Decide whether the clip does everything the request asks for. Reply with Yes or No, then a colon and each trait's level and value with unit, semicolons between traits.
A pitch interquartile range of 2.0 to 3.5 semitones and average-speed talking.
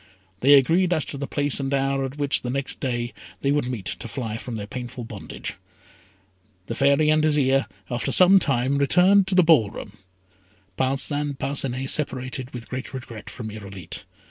Yes: average, 2.8 semitones; average, 170 wpm